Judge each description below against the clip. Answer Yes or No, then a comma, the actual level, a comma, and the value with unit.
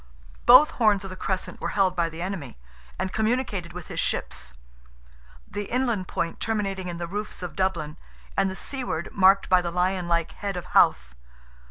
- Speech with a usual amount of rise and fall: Yes, average, 3.0 semitones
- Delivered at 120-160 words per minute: No, average, 180 wpm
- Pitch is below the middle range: No, high, 190 Hz